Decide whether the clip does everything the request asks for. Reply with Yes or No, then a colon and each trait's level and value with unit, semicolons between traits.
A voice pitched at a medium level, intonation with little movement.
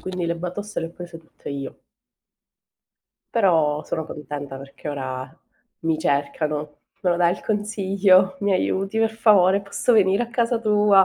No: medium, 180 Hz; average, 5.2 semitones